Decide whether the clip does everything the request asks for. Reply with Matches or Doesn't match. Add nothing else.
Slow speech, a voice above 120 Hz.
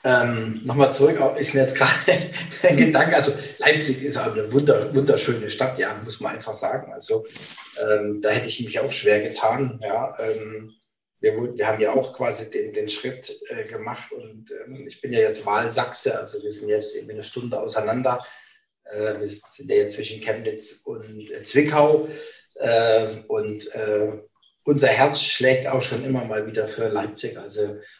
Doesn't match